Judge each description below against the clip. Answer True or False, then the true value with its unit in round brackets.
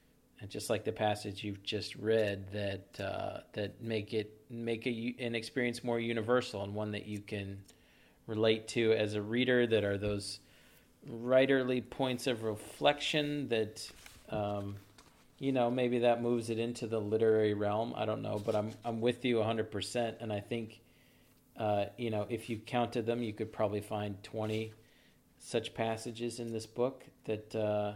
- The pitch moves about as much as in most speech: False (2.2 semitones)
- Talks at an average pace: True (170 wpm)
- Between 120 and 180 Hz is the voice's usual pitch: False (110 Hz)